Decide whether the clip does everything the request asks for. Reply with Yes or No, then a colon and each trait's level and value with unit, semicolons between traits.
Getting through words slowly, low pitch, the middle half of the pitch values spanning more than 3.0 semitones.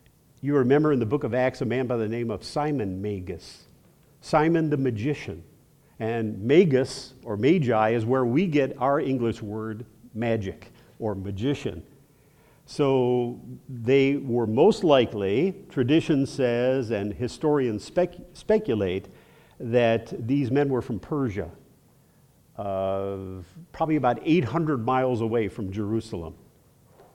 Yes: slow, 125 wpm; low, 125 Hz; average, 4.2 semitones